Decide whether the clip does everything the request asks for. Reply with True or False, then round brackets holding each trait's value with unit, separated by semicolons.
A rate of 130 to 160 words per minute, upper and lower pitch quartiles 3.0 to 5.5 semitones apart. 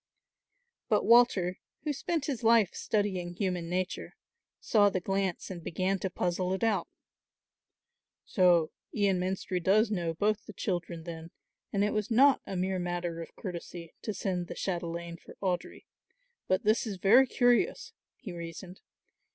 True (150 wpm; 3.4 semitones)